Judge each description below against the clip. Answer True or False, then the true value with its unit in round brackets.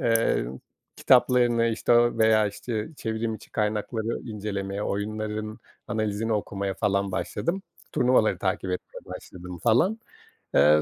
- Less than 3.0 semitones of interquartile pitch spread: True (2.5 semitones)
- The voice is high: False (110 Hz)